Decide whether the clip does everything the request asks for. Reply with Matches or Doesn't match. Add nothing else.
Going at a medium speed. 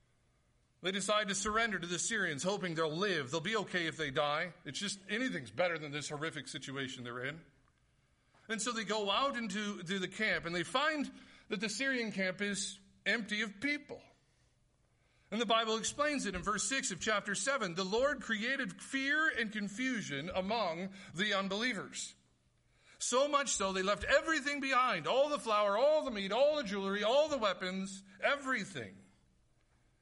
Matches